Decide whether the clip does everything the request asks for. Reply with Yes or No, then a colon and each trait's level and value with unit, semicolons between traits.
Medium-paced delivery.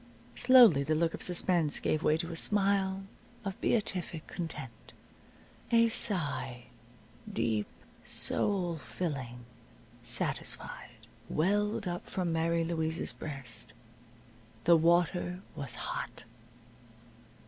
No: slow, 100 wpm